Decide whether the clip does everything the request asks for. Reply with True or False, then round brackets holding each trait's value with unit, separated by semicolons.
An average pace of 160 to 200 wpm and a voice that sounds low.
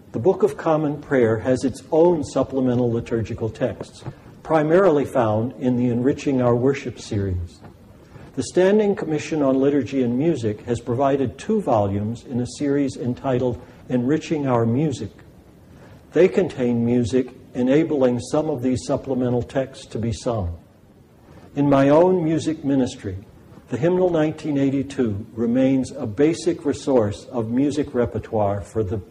False (135 wpm; 130 Hz)